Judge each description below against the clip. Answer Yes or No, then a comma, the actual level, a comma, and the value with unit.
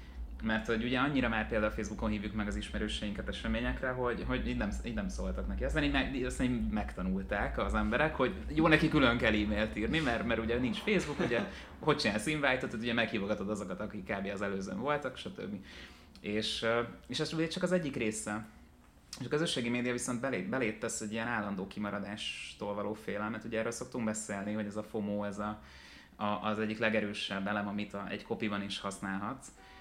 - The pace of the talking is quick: Yes, fast, 185 wpm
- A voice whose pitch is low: Yes, low, 110 Hz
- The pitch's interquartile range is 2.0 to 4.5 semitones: Yes, average, 3.1 semitones